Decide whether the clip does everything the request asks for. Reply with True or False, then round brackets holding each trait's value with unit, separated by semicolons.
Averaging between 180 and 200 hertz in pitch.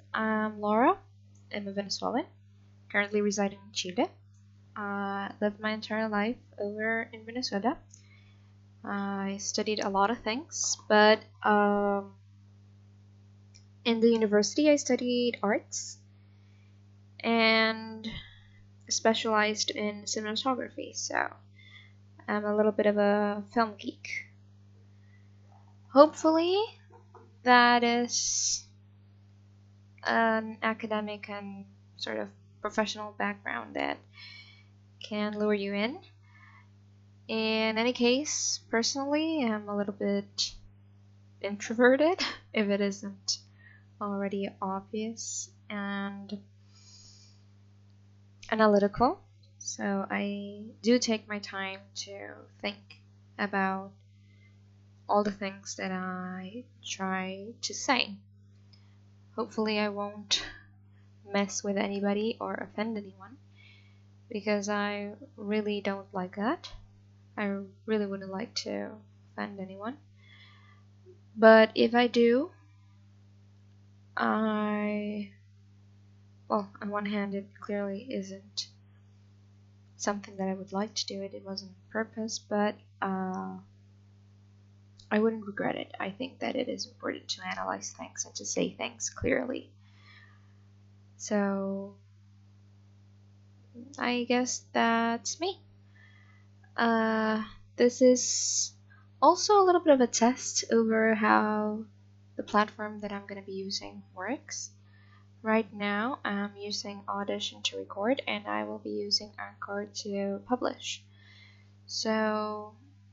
False (105 Hz)